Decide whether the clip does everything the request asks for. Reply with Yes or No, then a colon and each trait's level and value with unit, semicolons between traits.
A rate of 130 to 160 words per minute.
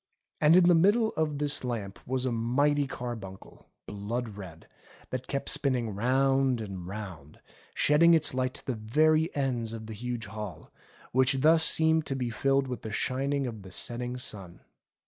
No: average, 170 wpm